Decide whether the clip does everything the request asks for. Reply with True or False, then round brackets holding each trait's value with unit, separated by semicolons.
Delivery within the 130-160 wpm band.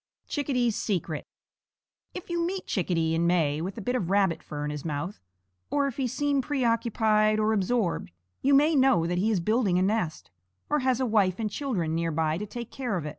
False (205 wpm)